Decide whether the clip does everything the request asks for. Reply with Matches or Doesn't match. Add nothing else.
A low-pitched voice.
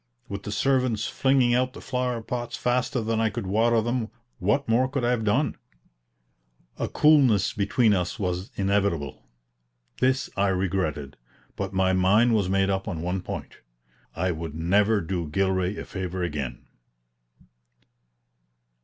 Matches